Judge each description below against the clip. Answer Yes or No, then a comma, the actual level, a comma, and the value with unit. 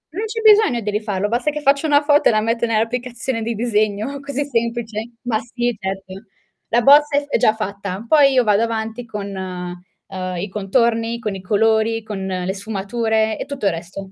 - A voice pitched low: No, high, 225 Hz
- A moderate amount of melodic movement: Yes, average, 3.6 semitones